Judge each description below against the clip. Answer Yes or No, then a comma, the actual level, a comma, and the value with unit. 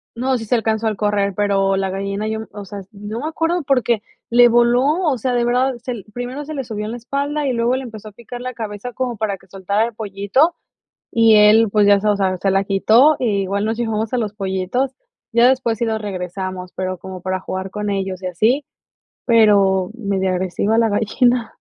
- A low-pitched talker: No, high, 215 Hz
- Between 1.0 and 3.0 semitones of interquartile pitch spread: No, average, 3.5 semitones